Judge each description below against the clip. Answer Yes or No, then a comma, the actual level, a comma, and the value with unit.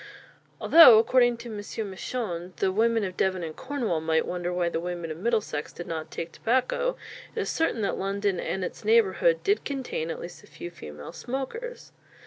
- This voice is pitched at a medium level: No, high, 200 Hz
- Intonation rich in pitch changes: Yes, wide, 6.7 semitones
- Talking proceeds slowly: No, average, 185 wpm